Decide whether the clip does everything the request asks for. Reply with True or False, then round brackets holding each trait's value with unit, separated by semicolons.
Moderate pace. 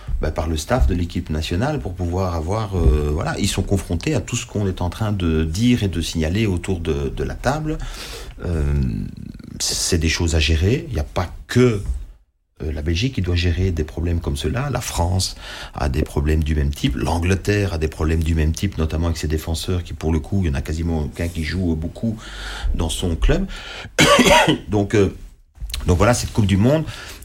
True (210 wpm)